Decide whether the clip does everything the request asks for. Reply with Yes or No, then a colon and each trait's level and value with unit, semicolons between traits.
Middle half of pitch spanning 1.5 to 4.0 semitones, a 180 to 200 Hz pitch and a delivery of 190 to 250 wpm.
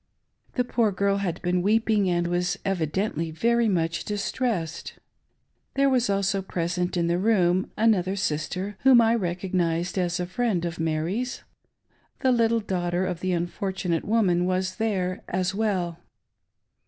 No: average, 3.5 semitones; medium, 185 Hz; average, 145 wpm